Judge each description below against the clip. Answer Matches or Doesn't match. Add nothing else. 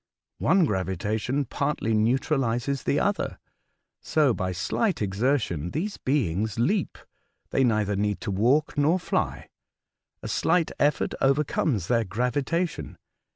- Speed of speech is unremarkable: Doesn't match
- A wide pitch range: Matches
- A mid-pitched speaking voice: Doesn't match